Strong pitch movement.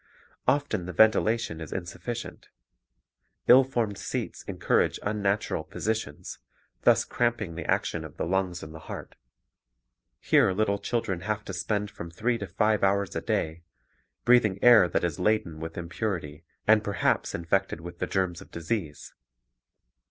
No: average, 4.3 semitones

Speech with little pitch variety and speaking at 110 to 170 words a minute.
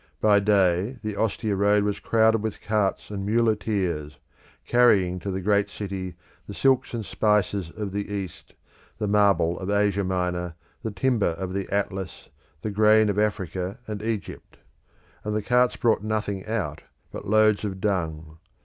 Yes: narrow, 2.3 semitones; average, 160 wpm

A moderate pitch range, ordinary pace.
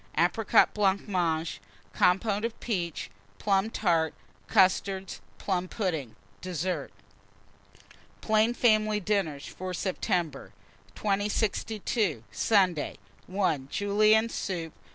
No: average, 3.6 semitones; slow, 90 wpm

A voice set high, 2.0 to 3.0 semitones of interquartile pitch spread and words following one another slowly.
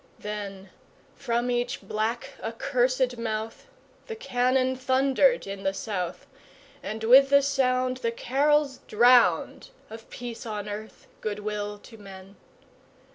No: high, 235 Hz; average, 3.6 semitones; slow, 125 wpm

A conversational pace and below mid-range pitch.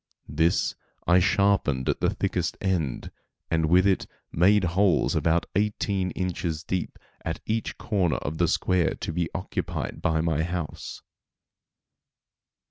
No: slow, 130 wpm; very low, 90 Hz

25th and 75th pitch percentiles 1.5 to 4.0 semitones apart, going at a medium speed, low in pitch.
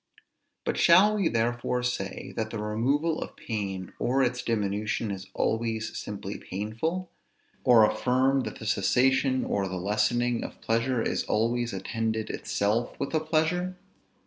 Yes: average, 3.7 semitones; average, 145 wpm; low, 115 Hz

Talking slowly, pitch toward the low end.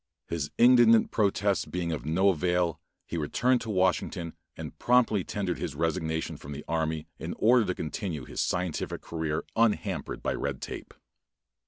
No: average, 155 wpm; very low, 90 Hz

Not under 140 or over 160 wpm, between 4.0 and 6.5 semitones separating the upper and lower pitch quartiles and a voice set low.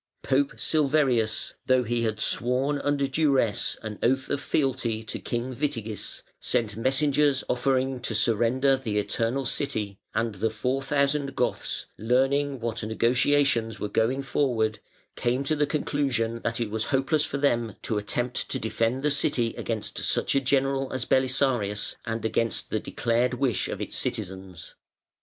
No: average, 150 wpm; average, 3.4 semitones; low, 125 Hz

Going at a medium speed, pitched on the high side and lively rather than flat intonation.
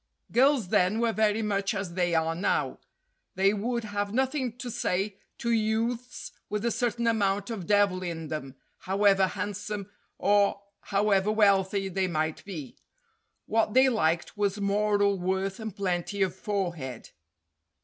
No: average, 145 wpm; high, 200 Hz; average, 2.7 semitones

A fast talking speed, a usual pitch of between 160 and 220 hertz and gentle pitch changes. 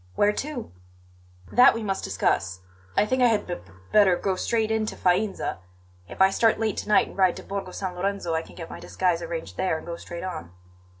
No: fast, 225 wpm; high, 190 Hz; average, 3.7 semitones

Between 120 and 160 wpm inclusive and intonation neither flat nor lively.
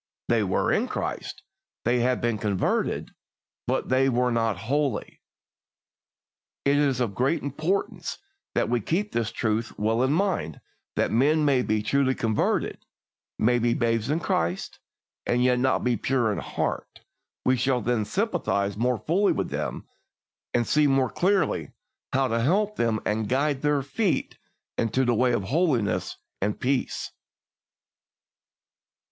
Yes: average, 150 wpm; average, 4.0 semitones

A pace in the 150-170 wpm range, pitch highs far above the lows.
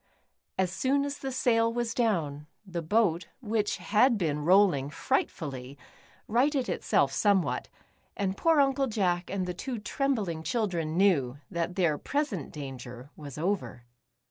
No: average, 140 wpm; wide, 6.7 semitones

